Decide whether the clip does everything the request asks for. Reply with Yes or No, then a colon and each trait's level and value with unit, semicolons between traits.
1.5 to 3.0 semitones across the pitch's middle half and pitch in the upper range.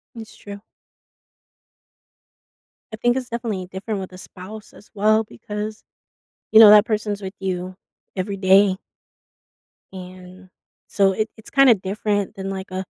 Yes: narrow, 2.4 semitones; high, 200 Hz